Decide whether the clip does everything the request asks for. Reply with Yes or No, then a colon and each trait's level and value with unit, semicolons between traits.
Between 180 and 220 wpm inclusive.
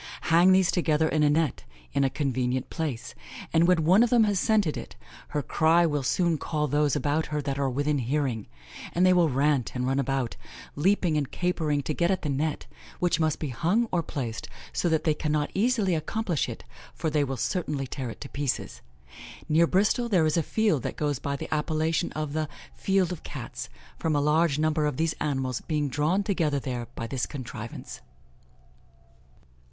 Yes: average, 195 wpm